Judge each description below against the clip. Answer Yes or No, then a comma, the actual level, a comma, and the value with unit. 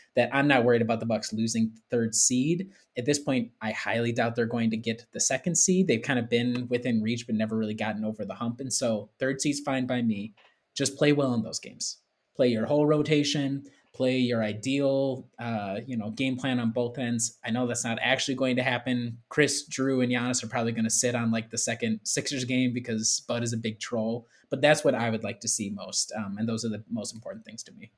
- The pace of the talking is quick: Yes, fast, 240 wpm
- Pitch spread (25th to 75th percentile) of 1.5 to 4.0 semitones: Yes, average, 2.8 semitones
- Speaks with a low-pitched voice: Yes, low, 120 Hz